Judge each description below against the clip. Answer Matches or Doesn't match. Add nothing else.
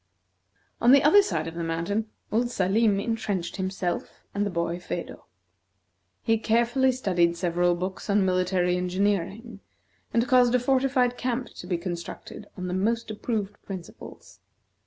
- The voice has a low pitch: Doesn't match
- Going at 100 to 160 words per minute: Matches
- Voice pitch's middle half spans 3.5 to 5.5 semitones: Matches